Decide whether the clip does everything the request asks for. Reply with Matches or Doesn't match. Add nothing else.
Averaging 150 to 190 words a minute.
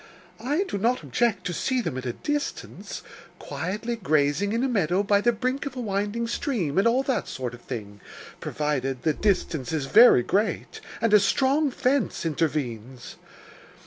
Matches